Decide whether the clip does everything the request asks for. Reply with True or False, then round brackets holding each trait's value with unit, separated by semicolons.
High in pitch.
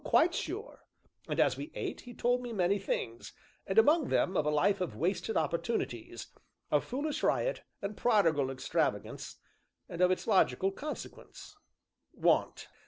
True (200 Hz)